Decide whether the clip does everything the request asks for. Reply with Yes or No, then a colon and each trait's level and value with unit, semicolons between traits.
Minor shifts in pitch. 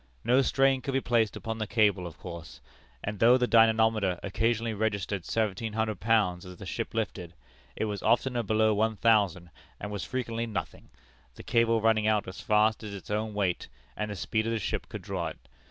Yes: narrow, 2.3 semitones